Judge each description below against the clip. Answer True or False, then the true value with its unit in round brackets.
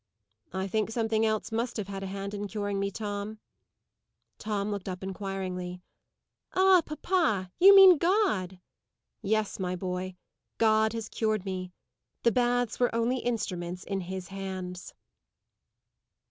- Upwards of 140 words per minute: False (135 wpm)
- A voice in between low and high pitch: False (205 Hz)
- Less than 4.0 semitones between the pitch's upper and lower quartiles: True (3.3 semitones)